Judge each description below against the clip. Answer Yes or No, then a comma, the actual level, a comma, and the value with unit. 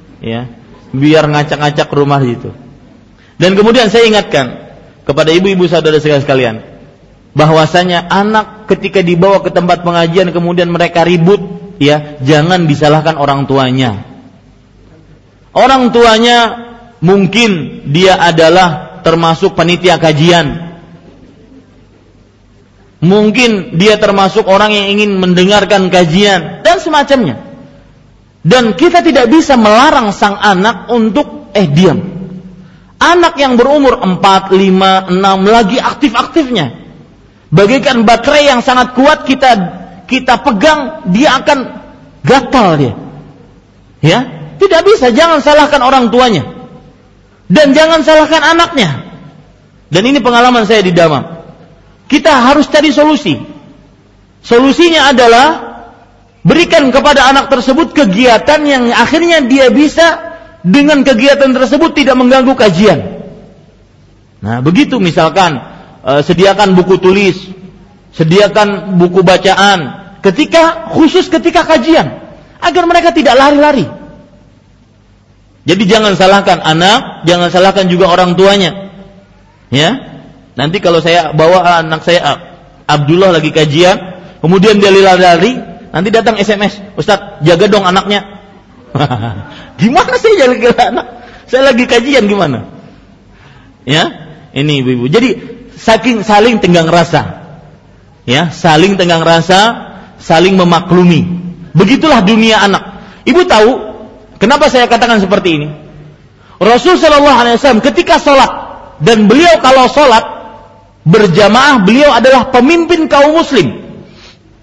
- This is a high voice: Yes, high, 195 Hz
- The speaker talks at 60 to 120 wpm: Yes, average, 110 wpm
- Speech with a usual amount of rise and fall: No, wide, 7.4 semitones